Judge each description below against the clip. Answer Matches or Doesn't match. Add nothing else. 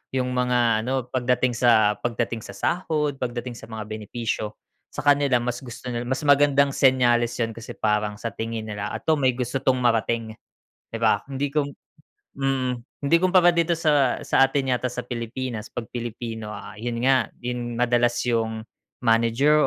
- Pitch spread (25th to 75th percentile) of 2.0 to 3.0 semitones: Matches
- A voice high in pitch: Doesn't match